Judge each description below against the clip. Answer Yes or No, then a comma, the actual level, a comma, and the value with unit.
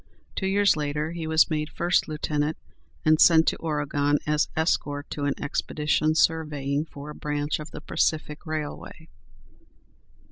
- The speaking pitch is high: No, medium, 150 Hz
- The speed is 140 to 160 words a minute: Yes, average, 145 wpm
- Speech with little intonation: Yes, narrow, 1.4 semitones